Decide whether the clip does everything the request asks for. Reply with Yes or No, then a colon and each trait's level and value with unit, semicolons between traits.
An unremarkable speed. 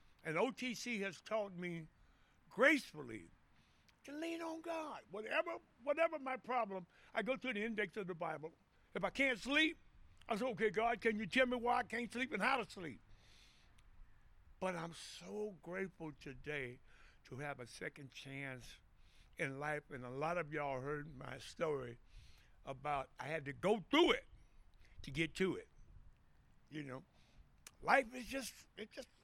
Yes: average, 165 wpm